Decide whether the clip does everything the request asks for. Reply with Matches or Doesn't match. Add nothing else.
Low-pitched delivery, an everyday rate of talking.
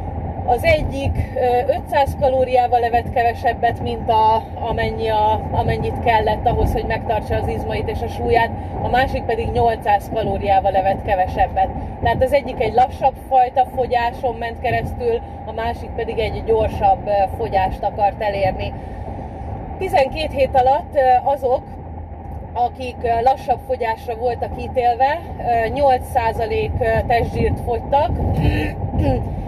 Doesn't match